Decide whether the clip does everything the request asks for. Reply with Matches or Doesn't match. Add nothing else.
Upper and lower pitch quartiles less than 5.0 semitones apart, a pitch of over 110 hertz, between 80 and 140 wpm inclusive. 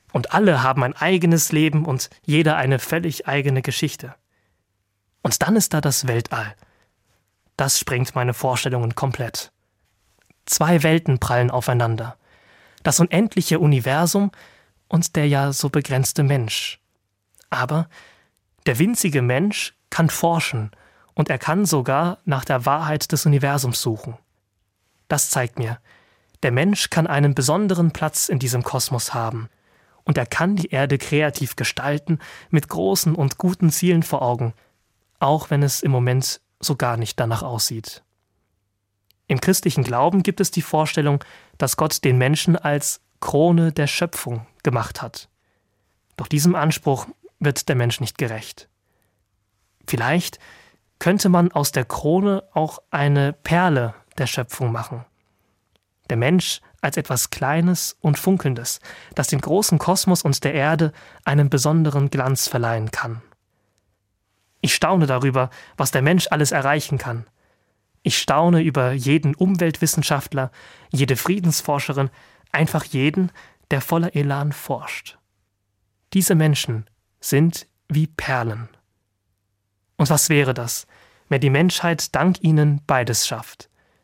Doesn't match